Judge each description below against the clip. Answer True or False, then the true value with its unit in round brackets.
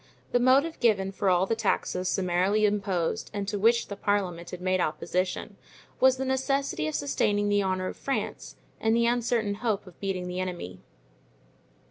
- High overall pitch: True (200 Hz)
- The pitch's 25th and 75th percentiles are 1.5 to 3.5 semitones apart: False (3.9 semitones)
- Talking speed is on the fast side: False (170 wpm)